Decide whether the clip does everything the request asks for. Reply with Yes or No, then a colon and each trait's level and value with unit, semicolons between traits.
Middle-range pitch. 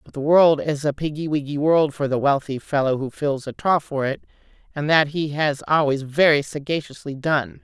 Yes: medium, 145 Hz